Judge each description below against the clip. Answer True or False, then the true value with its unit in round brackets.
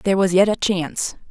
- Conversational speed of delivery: False (230 wpm)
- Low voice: False (190 Hz)